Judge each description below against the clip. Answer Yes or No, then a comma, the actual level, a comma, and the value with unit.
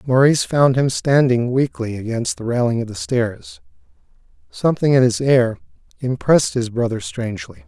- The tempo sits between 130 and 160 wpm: Yes, average, 150 wpm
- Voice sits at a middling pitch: No, low, 125 Hz